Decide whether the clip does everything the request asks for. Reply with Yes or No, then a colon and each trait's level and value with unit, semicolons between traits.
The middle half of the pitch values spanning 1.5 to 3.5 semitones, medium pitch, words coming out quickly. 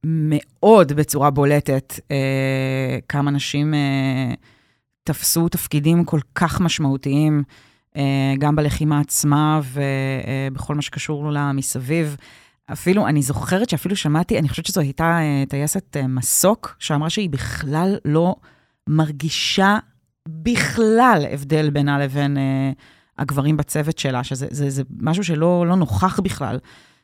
No: average, 2.9 semitones; medium, 145 Hz; average, 125 wpm